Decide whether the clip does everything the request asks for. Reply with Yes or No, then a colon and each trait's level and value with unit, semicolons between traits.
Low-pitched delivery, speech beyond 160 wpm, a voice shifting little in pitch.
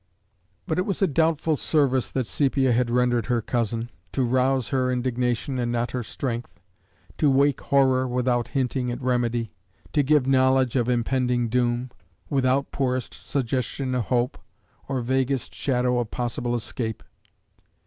No: low, 125 Hz; average, 150 wpm; narrow, 1.8 semitones